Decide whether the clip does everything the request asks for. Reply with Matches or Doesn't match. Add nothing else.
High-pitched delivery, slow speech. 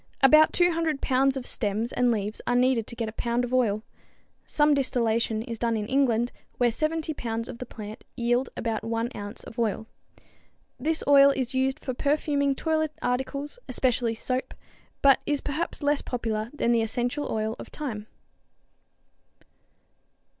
Doesn't match